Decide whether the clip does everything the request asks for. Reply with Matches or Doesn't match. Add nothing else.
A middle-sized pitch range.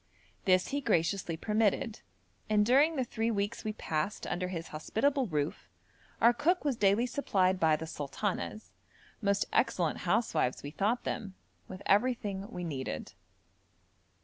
Matches